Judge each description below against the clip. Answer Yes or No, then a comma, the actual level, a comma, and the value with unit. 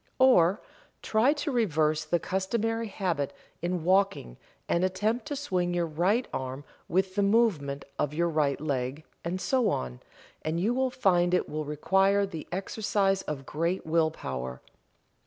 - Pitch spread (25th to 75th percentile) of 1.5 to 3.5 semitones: No, average, 4.7 semitones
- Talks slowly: No, average, 155 wpm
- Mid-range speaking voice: Yes, medium, 175 Hz